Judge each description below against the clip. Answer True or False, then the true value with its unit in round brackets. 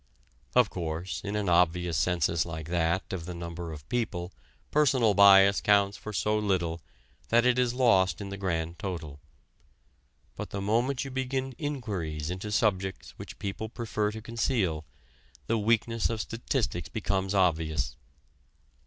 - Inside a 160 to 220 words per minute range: False (145 wpm)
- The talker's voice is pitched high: False (100 Hz)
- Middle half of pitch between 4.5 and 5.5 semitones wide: True (4.8 semitones)